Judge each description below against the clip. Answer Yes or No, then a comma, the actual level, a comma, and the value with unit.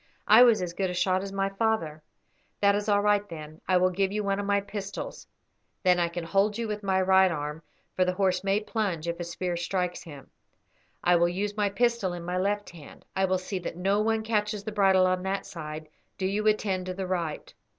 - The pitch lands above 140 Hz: Yes, high, 190 Hz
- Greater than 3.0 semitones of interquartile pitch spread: No, narrow, 2.5 semitones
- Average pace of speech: No, fast, 230 wpm